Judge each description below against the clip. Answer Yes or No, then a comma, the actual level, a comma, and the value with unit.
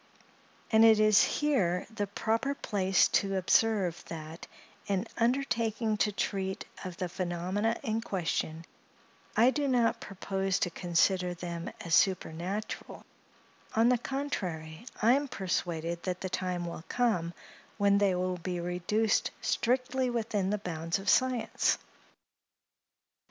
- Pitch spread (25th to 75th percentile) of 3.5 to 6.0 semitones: Yes, average, 4.2 semitones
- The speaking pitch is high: Yes, high, 195 Hz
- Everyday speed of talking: No, slow, 130 wpm